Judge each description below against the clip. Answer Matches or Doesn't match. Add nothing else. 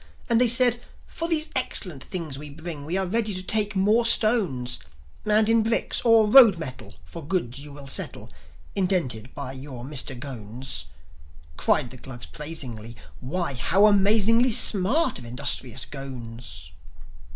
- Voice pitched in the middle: Matches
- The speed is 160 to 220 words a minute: Doesn't match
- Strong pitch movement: Matches